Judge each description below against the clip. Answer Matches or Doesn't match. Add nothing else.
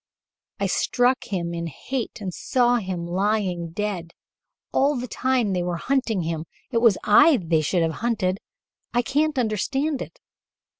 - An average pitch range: Doesn't match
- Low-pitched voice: Doesn't match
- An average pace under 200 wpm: Matches